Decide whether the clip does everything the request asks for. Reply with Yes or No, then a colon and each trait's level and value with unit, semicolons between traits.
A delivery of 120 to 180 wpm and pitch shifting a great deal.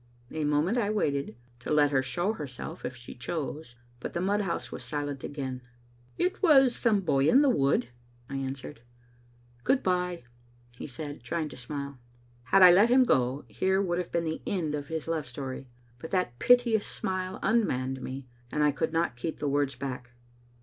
No: average, 190 wpm; wide, 5.7 semitones